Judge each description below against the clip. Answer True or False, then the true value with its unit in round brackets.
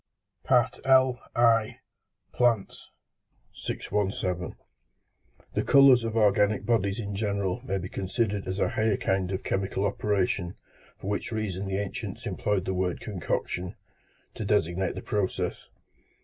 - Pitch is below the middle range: True (100 Hz)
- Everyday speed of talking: False (130 wpm)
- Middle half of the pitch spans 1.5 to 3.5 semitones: True (2.6 semitones)